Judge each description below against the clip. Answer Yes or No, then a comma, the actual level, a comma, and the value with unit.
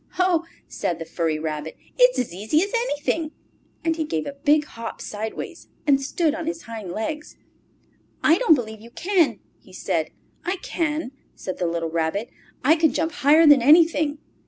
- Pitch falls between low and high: No, very high, 290 Hz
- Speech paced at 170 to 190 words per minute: Yes, average, 175 wpm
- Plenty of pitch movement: Yes, wide, 7.3 semitones